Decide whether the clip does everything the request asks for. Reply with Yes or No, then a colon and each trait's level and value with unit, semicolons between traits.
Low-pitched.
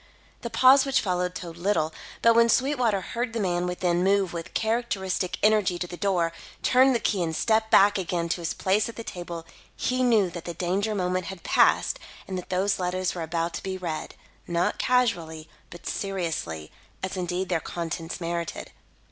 No: medium, 185 Hz